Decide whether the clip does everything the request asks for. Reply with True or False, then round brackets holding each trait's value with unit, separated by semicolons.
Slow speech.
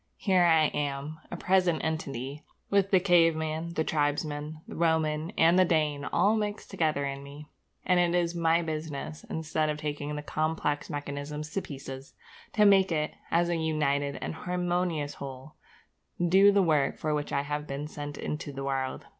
False (175 wpm)